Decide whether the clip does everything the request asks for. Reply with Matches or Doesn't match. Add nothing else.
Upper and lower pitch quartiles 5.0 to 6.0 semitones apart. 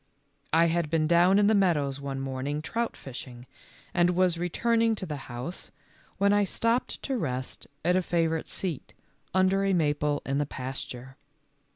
Matches